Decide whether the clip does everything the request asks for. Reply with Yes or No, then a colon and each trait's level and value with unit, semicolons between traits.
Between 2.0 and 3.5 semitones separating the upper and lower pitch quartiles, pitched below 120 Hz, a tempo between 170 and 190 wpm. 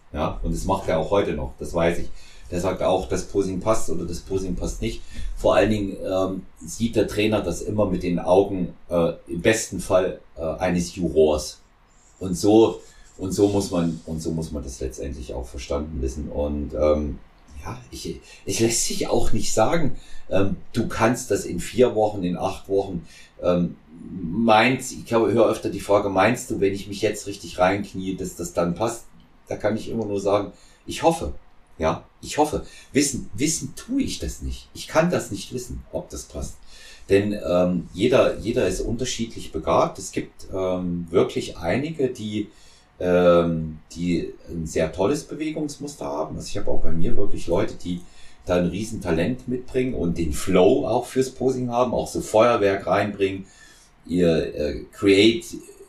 No: average, 4.5 semitones; very low, 95 Hz; average, 185 wpm